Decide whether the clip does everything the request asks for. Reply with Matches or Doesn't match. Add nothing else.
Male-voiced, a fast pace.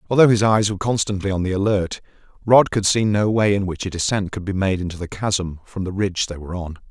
Matches